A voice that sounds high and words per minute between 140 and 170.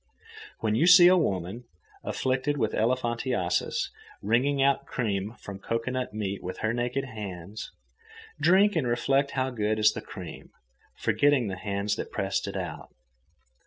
No: low, 120 Hz; average, 145 wpm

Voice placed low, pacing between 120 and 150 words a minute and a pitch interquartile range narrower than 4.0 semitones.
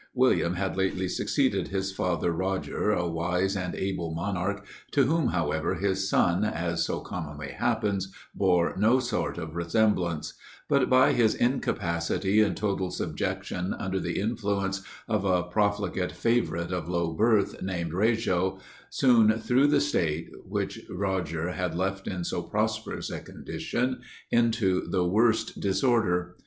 Yes: very low, 95 Hz; average, 140 wpm; average, 3.5 semitones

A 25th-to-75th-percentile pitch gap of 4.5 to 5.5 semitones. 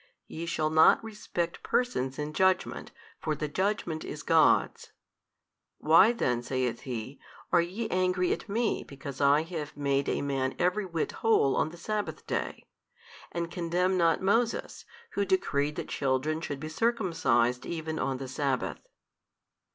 Yes: average, 4.8 semitones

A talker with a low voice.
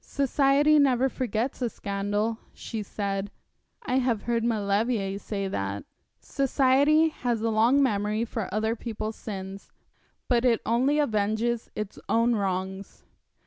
No: high, 225 Hz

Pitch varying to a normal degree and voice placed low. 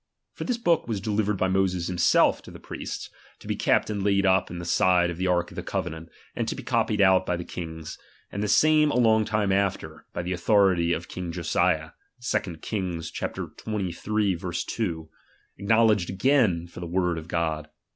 Yes: average, 3.4 semitones; very low, 95 Hz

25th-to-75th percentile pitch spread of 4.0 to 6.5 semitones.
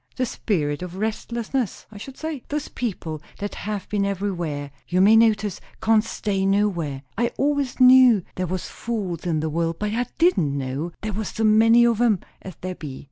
Yes: average, 5.0 semitones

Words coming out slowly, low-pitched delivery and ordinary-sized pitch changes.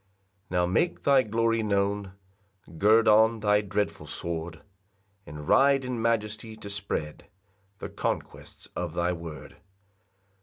Yes: slow, 125 wpm; low, 105 Hz; average, 4.1 semitones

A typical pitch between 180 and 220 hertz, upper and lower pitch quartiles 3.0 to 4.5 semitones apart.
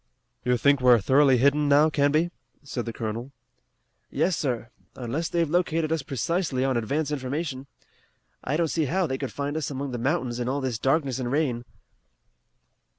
No: medium, 140 Hz; average, 3.6 semitones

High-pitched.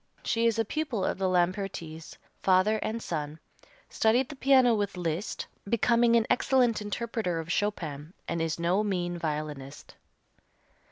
Yes: high, 195 Hz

